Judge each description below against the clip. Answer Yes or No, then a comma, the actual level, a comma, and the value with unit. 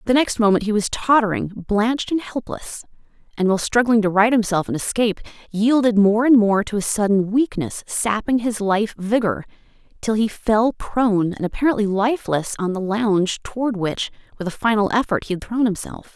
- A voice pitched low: No, high, 215 Hz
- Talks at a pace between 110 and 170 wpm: No, average, 185 wpm